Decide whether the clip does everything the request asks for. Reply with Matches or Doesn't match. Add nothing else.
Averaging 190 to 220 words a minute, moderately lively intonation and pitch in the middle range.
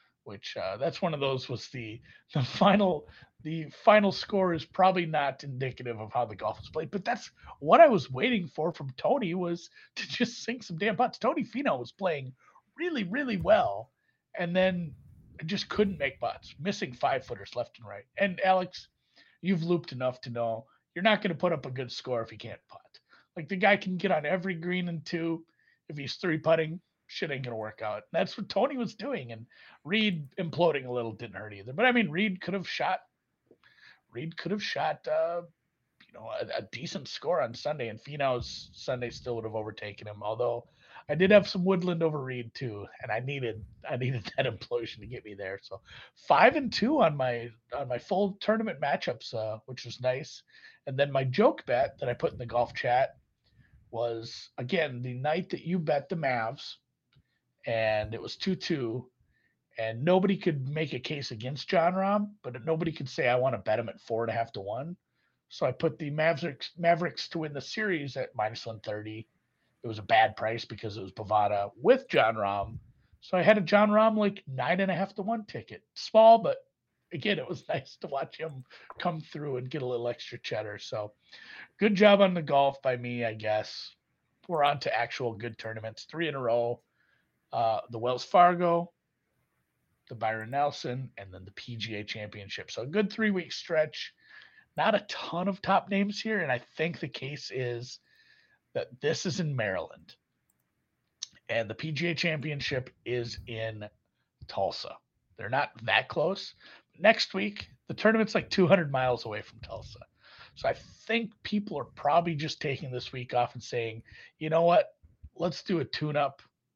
Doesn't match